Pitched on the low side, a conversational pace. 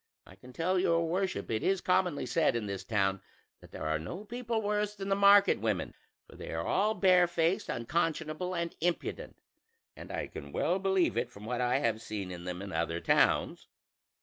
No: medium, 165 Hz; average, 195 wpm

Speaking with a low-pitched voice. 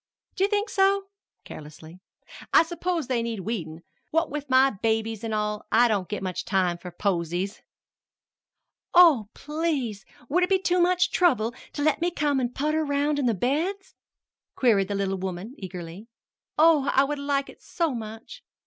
No: very high, 250 Hz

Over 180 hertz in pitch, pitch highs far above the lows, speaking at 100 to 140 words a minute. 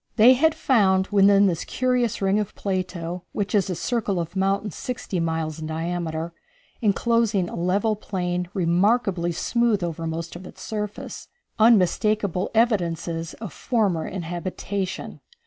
No: high, 190 Hz; average, 3.7 semitones; slow, 135 wpm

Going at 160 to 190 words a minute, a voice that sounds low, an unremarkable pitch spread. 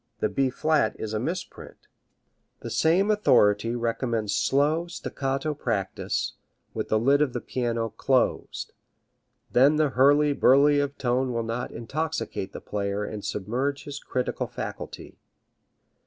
No: slow, 135 wpm; low, 130 Hz; average, 4.0 semitones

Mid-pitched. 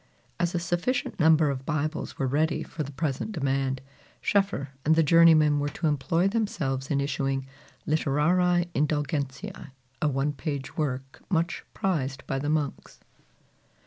Yes: medium, 150 Hz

